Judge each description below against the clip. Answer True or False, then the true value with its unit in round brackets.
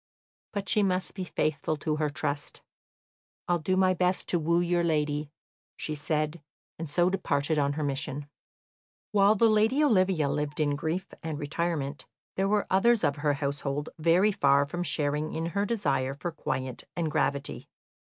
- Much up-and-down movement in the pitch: False (4.2 semitones)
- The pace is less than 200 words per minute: True (165 wpm)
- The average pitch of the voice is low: False (155 Hz)